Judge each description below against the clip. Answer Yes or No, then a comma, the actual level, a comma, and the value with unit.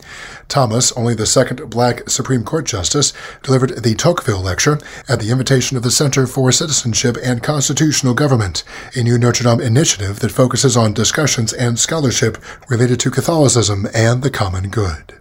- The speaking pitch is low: Yes, low, 125 Hz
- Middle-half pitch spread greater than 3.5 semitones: No, average, 2.8 semitones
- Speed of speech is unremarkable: Yes, average, 160 wpm